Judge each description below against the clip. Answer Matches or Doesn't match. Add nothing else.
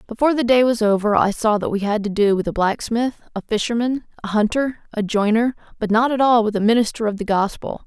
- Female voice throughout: Matches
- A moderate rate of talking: Doesn't match